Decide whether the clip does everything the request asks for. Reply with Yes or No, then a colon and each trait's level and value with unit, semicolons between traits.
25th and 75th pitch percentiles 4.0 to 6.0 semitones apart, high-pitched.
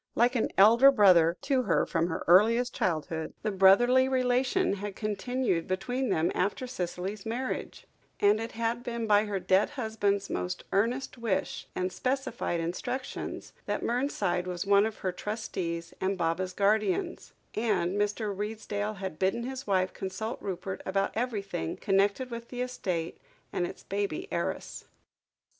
Yes: average, 4.3 semitones; high, 205 Hz